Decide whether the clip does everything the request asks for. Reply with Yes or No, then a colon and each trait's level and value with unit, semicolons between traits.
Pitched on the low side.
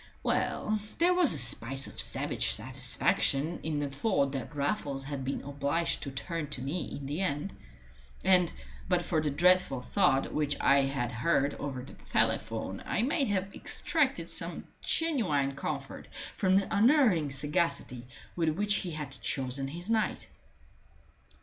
No: medium, 150 Hz